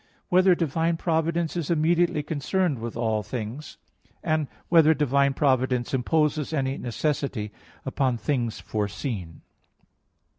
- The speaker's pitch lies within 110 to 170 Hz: Yes, medium, 140 Hz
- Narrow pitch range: No, average, 4.9 semitones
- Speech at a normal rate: No, slow, 115 wpm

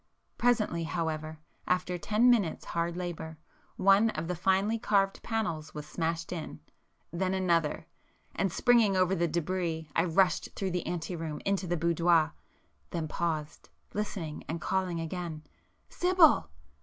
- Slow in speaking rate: Yes, slow, 130 wpm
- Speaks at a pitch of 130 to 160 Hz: No, medium, 175 Hz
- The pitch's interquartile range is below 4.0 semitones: Yes, average, 3.0 semitones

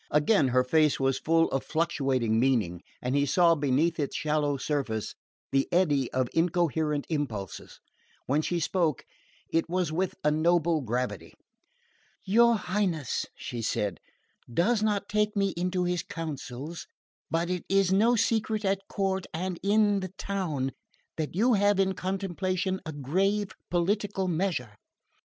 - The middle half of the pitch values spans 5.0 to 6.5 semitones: Yes, average, 5.3 semitones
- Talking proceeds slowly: No, average, 145 wpm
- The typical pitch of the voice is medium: Yes, medium, 170 Hz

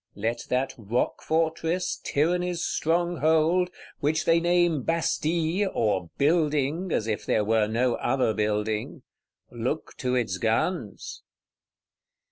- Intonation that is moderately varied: No, wide, 6.8 semitones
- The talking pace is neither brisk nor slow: No, slow, 105 wpm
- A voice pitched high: No, medium, 150 Hz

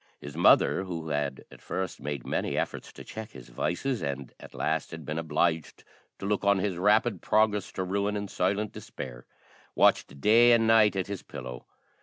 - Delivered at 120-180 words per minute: No, average, 190 wpm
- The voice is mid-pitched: No, very low, 95 Hz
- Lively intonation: Yes, wide, 5.9 semitones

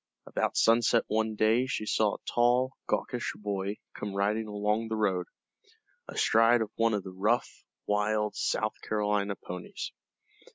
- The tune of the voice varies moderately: No, narrow, 1.8 semitones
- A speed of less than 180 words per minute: Yes, average, 140 wpm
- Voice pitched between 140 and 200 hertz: No, low, 110 Hz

